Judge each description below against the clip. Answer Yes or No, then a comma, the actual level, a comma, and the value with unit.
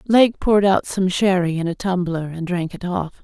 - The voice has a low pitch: No, medium, 185 Hz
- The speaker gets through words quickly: Yes, fast, 225 wpm